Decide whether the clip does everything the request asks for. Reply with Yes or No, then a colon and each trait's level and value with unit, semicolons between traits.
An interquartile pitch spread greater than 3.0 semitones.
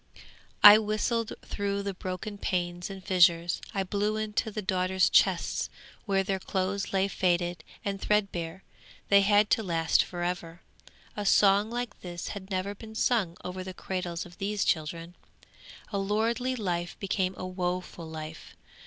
No: narrow, 2.6 semitones